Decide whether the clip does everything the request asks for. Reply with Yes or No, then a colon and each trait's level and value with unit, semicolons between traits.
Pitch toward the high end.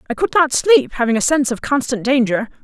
Yes: very high, 265 Hz